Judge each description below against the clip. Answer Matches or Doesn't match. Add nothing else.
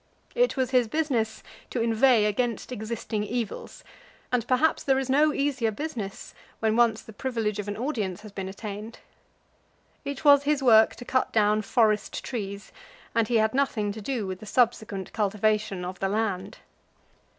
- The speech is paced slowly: Doesn't match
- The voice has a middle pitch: Doesn't match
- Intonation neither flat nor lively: Matches